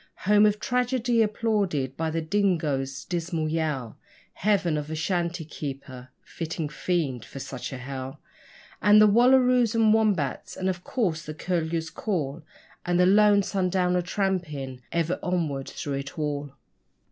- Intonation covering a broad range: Yes, wide, 5.8 semitones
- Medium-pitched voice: Yes, medium, 170 Hz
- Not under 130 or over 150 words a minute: Yes, average, 145 wpm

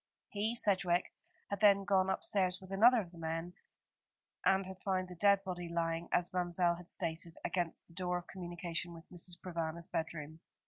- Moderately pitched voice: Yes, medium, 180 Hz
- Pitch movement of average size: No, narrow, 2.1 semitones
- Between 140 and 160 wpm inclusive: No, average, 175 wpm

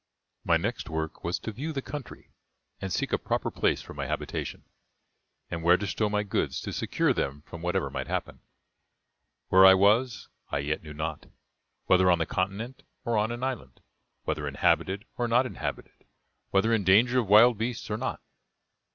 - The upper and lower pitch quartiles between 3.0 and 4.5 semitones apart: No, average, 5.1 semitones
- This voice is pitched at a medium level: No, low, 100 Hz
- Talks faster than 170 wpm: Yes, average, 180 wpm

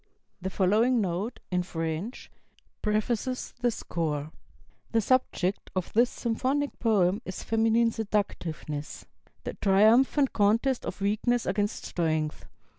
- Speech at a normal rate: No, slow, 115 wpm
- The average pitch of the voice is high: Yes, high, 210 Hz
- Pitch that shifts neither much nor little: Yes, average, 4.7 semitones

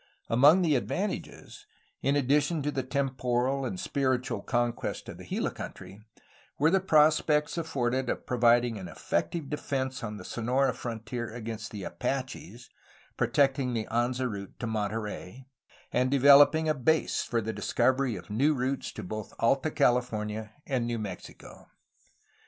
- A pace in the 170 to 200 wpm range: No, average, 145 wpm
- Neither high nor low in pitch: No, low, 125 Hz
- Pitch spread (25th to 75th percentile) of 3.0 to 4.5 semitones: Yes, average, 3.5 semitones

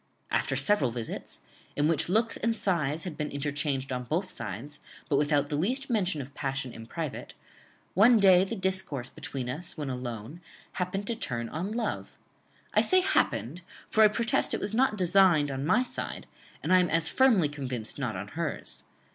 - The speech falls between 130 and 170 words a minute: No, average, 180 wpm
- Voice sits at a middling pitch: Yes, medium, 155 Hz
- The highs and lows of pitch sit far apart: Yes, wide, 6.5 semitones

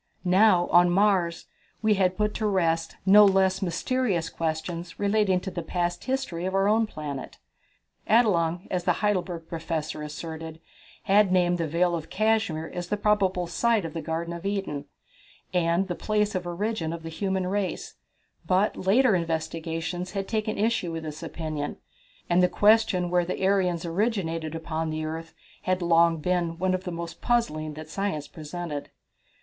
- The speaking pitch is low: No, medium, 175 Hz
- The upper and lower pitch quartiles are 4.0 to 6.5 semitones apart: No, average, 3.3 semitones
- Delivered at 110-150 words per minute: No, average, 165 wpm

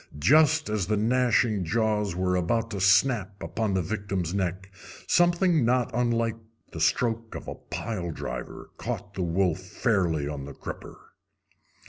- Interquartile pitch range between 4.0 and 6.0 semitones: Yes, average, 4.3 semitones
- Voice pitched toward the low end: Yes, low, 105 Hz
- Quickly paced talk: No, average, 145 wpm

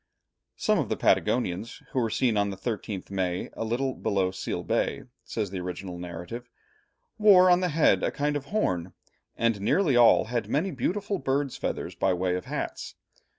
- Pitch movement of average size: No, wide, 7.2 semitones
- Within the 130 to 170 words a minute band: No, average, 180 wpm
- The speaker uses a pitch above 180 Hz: No, low, 115 Hz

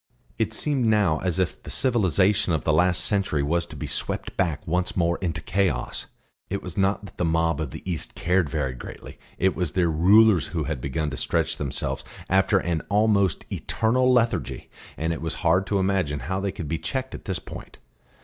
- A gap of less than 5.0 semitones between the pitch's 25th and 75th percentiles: Yes, average, 3.6 semitones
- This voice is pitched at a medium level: No, very low, 90 Hz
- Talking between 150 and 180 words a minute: No, average, 200 wpm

